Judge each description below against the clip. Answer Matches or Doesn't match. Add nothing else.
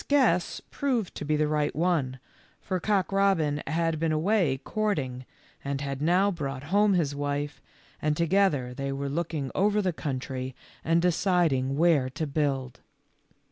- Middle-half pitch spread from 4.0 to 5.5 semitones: Matches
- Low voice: Doesn't match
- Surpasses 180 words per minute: Doesn't match